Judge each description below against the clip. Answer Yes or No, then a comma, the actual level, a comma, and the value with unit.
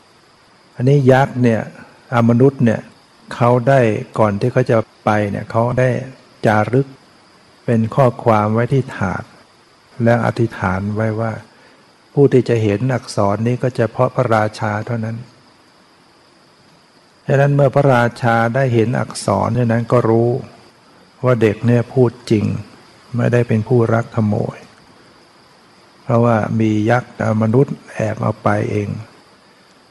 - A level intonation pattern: Yes, narrow, 2.3 semitones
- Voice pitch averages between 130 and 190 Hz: No, low, 115 Hz